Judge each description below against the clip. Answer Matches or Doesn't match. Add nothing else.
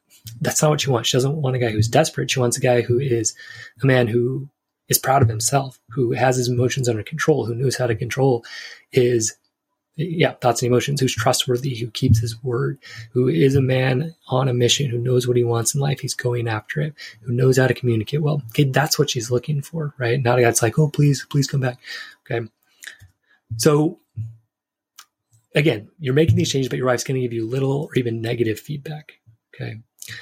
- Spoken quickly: Matches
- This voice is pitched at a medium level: Doesn't match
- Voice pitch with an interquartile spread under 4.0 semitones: Matches